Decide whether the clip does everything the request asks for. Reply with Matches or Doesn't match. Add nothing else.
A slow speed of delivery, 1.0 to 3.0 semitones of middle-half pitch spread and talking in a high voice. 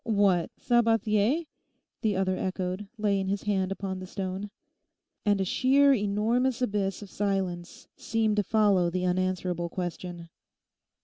Matches